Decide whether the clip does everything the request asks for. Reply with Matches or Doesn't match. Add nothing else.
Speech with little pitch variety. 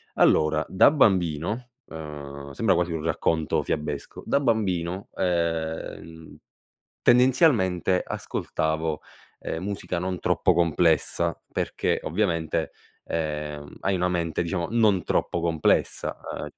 Doesn't match